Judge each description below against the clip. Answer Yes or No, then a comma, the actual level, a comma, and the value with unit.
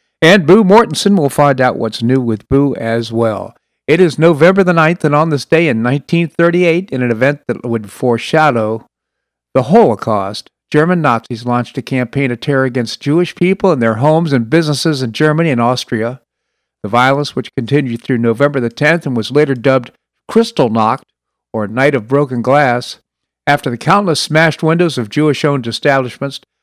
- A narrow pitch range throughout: No, average, 4.8 semitones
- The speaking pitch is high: No, medium, 140 Hz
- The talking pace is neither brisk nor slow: Yes, average, 175 wpm